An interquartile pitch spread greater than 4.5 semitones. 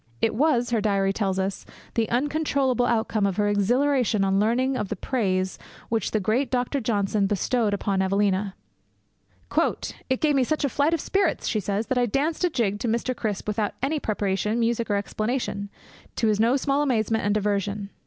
No: average, 4.1 semitones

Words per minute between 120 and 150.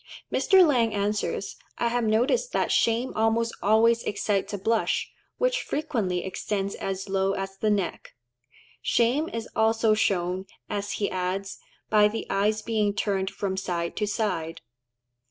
Yes: average, 145 wpm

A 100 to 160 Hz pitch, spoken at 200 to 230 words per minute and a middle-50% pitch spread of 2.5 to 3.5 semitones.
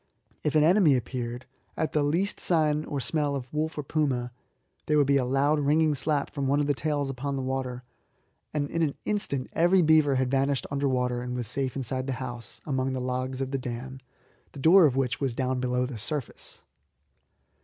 Yes: low, 135 Hz; fast, 205 wpm; average, 2.8 semitones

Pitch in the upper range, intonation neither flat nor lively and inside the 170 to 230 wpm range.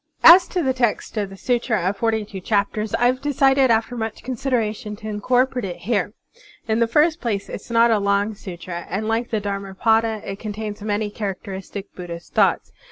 Yes: high, 220 Hz; average, 3.0 semitones; average, 195 wpm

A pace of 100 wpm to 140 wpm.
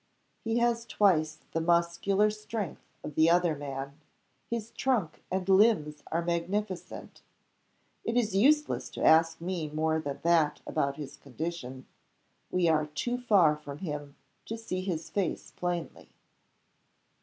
Yes: slow, 135 wpm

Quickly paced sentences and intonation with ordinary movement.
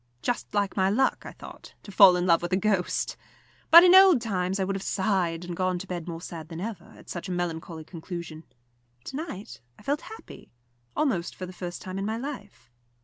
Yes: fast, 215 wpm; average, 3.6 semitones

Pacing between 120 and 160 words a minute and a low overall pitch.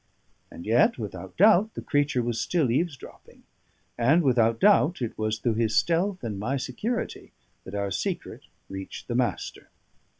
Yes: average, 155 wpm; low, 120 Hz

